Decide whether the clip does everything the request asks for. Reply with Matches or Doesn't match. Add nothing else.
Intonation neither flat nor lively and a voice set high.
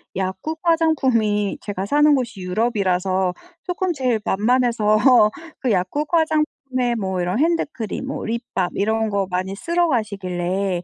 Doesn't match